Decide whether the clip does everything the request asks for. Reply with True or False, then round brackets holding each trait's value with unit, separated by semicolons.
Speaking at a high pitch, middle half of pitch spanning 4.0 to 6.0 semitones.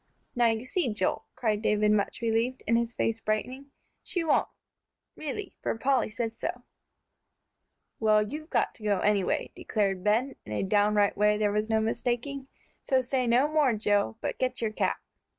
False (225 Hz; 3.5 semitones)